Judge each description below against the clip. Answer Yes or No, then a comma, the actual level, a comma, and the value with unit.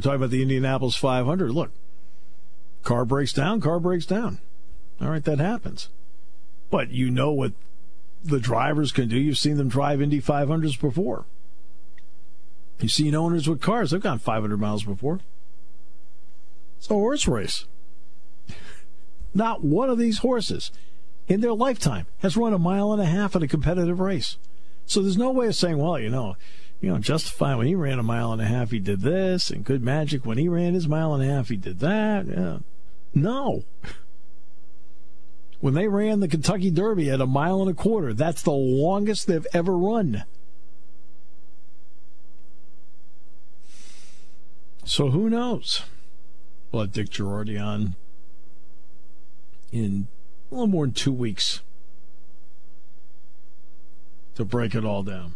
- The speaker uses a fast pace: No, average, 155 wpm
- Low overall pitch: Yes, low, 115 Hz